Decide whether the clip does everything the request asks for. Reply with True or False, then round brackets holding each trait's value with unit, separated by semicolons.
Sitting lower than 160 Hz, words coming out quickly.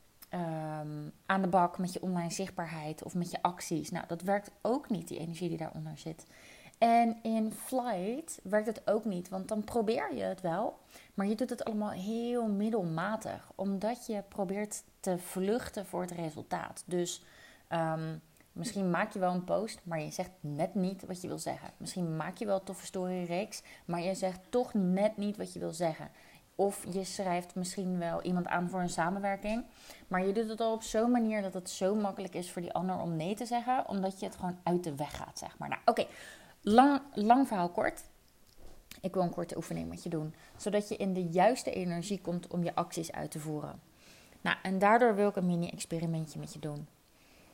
False (185 Hz; 205 wpm)